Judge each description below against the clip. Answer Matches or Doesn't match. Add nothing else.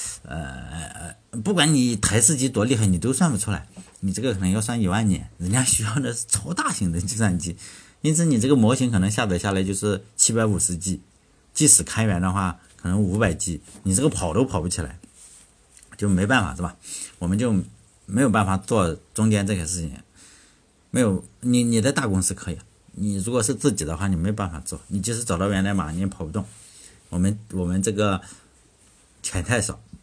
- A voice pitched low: Matches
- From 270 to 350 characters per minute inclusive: Matches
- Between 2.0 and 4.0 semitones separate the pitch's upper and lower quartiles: Matches